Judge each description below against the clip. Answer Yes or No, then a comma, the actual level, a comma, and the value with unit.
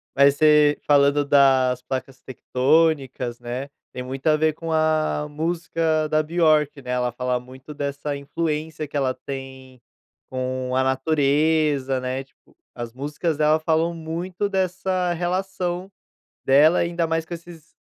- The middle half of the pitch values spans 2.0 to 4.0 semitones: Yes, average, 3.5 semitones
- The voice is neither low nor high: Yes, medium, 150 Hz